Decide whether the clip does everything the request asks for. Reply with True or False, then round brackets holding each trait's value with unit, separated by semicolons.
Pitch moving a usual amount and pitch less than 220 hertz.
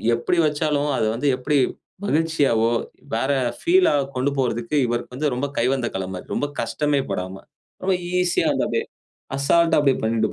True (4.3 semitones; 135 Hz)